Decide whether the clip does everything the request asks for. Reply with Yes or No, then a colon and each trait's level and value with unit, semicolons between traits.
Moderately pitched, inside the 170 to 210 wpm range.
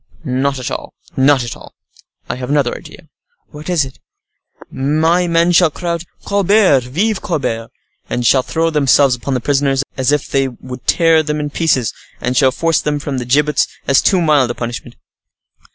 Yes: medium, 145 Hz; average, 180 wpm